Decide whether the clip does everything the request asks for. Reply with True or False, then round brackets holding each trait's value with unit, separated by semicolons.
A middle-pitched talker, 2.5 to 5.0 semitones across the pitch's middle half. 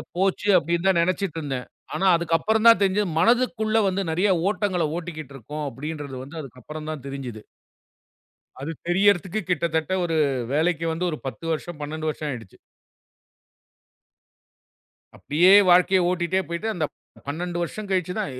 True (170 Hz; 3.8 semitones)